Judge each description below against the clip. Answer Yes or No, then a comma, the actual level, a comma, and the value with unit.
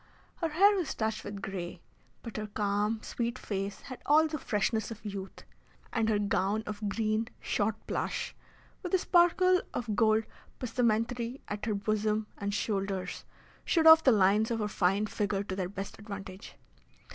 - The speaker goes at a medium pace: Yes, average, 165 wpm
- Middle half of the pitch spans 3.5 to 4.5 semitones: No, average, 2.8 semitones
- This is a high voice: Yes, high, 215 Hz